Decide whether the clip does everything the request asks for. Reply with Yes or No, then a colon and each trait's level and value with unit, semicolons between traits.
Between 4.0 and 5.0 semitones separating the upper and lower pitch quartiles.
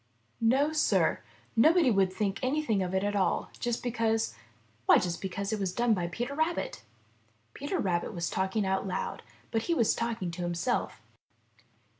Yes: average, 4.7 semitones